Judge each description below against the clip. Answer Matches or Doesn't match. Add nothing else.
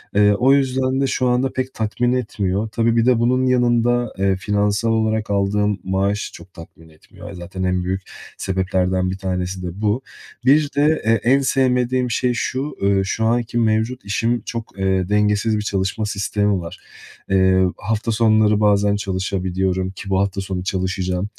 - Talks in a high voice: Doesn't match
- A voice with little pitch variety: Doesn't match